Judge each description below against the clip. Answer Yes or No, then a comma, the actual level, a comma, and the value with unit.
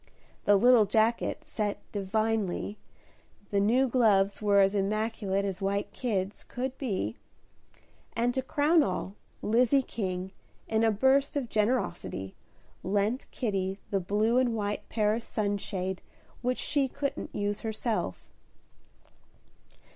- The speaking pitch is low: No, high, 215 Hz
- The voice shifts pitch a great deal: No, average, 3.5 semitones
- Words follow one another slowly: Yes, slow, 120 wpm